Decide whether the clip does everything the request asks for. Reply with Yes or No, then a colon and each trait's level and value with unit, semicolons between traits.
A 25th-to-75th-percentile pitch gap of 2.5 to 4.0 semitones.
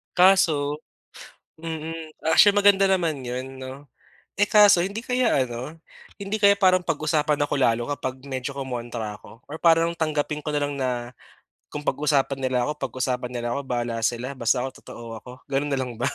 No: average, 4.6 semitones